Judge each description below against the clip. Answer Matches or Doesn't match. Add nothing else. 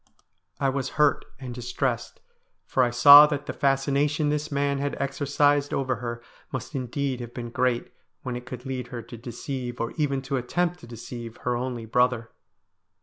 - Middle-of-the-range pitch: Doesn't match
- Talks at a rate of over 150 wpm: Matches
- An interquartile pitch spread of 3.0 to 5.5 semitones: Doesn't match